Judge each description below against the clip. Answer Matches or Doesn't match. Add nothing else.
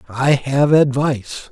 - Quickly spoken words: Doesn't match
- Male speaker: Matches